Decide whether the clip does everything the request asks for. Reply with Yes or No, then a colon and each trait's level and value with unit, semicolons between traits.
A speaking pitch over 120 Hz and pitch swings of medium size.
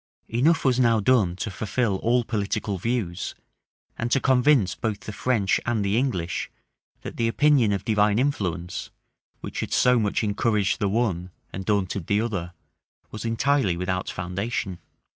No: low, 105 Hz; average, 3.9 semitones